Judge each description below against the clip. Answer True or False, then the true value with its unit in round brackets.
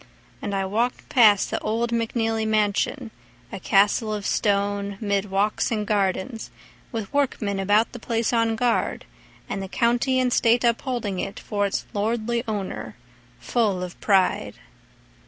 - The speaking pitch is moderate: False (215 Hz)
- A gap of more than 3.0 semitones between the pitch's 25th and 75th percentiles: False (2.6 semitones)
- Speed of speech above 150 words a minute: False (145 wpm)